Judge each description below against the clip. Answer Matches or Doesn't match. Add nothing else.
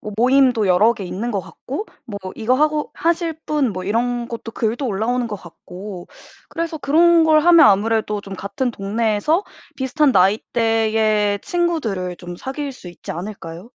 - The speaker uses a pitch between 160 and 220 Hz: Doesn't match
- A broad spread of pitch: Matches